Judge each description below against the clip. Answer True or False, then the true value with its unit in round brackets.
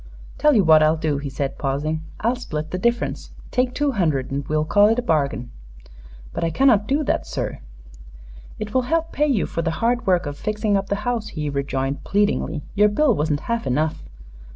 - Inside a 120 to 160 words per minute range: False (200 wpm)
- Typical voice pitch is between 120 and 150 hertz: False (185 Hz)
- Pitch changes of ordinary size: False (7.6 semitones)